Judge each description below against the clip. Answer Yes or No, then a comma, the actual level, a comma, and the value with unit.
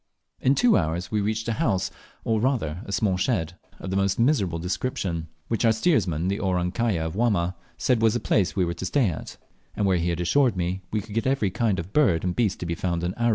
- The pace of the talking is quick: Yes, fast, 240 wpm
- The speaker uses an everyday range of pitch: Yes, average, 4.6 semitones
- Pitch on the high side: No, very low, 95 Hz